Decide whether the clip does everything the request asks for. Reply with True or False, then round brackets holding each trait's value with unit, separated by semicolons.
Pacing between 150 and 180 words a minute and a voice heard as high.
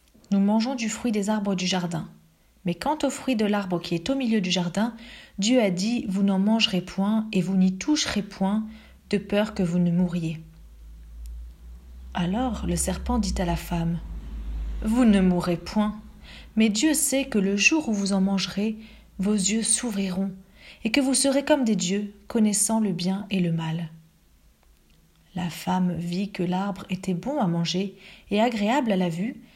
True (175 wpm; 195 Hz)